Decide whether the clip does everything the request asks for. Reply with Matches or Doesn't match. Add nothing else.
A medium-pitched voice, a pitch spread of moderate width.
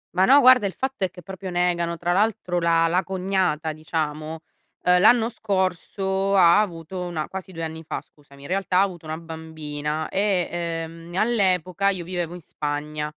Matches